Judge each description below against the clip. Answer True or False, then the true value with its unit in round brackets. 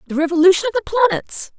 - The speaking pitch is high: True (360 Hz)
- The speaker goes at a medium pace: True (190 wpm)